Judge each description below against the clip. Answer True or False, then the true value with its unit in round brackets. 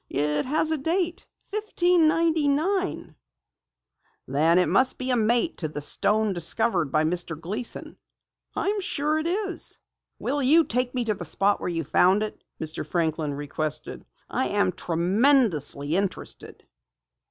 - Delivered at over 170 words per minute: False (140 wpm)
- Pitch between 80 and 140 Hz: False (215 Hz)